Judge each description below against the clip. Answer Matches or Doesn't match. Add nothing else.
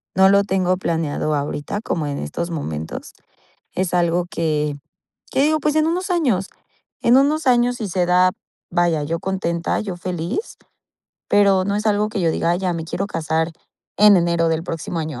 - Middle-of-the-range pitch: Matches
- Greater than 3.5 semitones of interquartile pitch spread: Matches